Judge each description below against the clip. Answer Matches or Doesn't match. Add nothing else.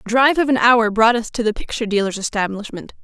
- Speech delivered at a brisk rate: Matches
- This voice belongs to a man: Doesn't match